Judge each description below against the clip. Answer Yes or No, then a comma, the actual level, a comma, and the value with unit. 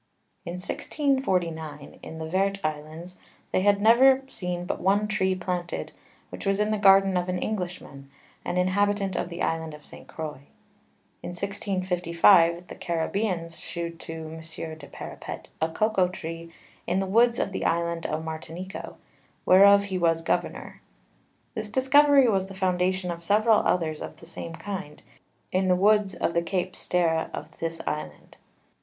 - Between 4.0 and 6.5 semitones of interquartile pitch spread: No, average, 3.2 semitones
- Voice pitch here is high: No, medium, 180 Hz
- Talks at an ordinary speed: Yes, average, 160 wpm